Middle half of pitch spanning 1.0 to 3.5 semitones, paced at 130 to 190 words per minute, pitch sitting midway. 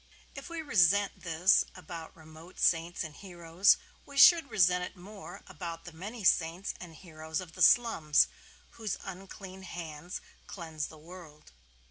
Yes: average, 3.2 semitones; average, 145 wpm; medium, 175 Hz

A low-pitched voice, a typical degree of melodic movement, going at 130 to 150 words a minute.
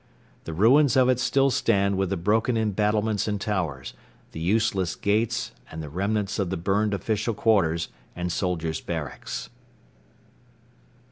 Yes: low, 105 Hz; average, 3.8 semitones; average, 140 wpm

